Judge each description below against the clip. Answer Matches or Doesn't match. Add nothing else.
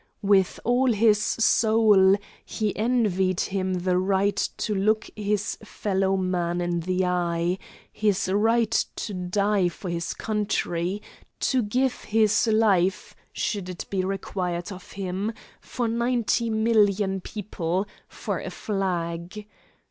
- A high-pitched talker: Matches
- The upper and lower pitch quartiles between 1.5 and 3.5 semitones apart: Matches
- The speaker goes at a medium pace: Doesn't match